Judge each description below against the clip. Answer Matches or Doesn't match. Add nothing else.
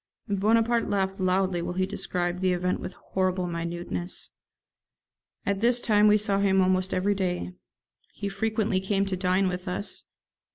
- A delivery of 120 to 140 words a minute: Doesn't match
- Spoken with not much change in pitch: Matches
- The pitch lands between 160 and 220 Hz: Matches